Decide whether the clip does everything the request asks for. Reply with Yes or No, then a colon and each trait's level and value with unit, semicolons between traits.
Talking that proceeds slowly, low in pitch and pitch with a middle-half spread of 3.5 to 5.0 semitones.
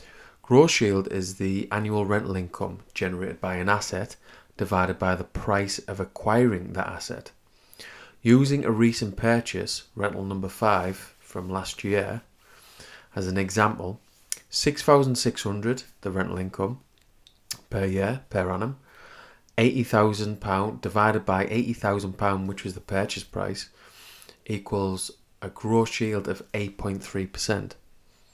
No: slow, 120 wpm; low, 100 Hz; narrow, 2.6 semitones